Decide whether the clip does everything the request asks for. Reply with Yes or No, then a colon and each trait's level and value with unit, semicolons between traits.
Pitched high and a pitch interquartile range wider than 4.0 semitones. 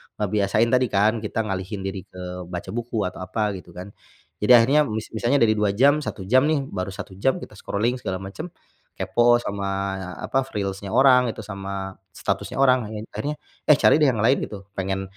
No: low, 105 Hz; average, 4.5 semitones